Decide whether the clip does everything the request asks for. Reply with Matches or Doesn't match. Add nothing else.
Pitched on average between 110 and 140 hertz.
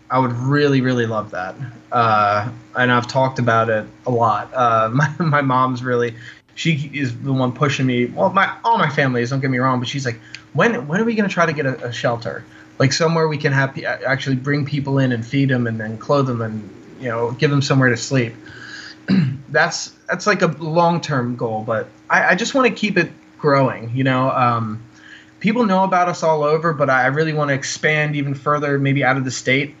Matches